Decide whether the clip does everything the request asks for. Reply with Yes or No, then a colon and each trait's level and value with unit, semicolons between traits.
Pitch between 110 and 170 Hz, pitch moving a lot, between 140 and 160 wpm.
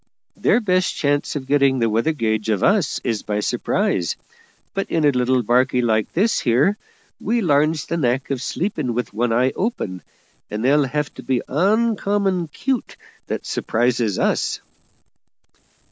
Yes: low, 135 Hz; wide, 6.4 semitones; average, 155 wpm